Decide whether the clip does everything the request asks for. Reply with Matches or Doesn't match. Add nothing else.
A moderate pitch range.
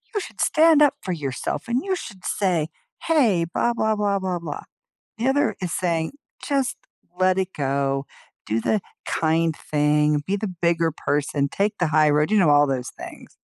Doesn't match